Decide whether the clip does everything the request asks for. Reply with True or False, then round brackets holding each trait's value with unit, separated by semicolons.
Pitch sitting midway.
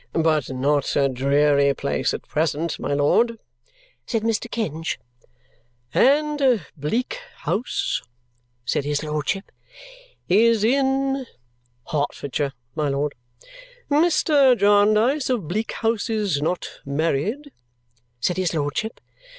True (180 Hz)